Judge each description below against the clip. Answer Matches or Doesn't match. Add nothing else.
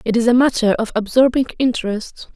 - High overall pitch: Matches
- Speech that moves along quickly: Doesn't match